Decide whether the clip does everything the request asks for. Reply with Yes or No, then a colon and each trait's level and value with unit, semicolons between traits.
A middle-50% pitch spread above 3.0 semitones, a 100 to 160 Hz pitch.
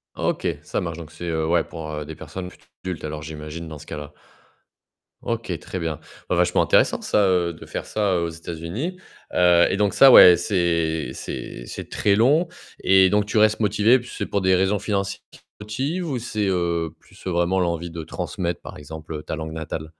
No: average, 4.1 semitones; very low, 85 Hz